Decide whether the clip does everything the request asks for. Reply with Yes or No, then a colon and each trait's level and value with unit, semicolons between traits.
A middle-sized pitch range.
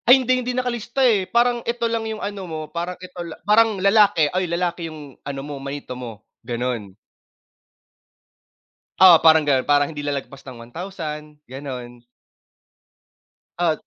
No: wide, 7.0 semitones